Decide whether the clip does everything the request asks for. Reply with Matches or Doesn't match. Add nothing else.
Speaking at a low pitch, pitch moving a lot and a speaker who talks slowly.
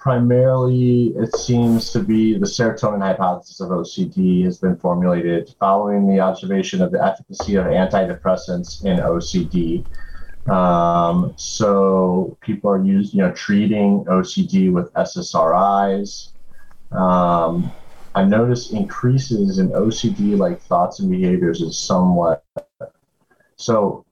Matches